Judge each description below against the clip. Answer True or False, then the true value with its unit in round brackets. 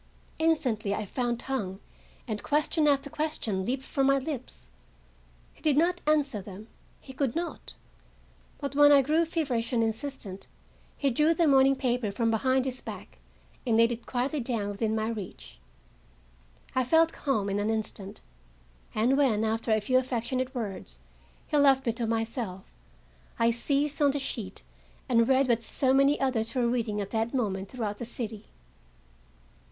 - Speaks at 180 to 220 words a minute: False (165 wpm)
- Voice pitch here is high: True (245 Hz)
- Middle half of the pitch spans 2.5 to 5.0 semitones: True (3.9 semitones)